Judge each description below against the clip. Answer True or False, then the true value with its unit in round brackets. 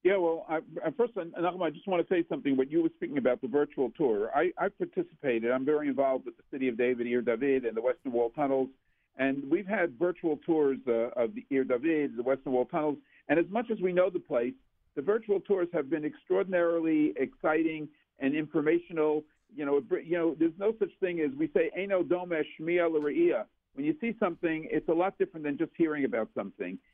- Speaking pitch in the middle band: True (160 Hz)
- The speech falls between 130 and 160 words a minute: False (205 wpm)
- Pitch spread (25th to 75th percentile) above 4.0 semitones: True (4.9 semitones)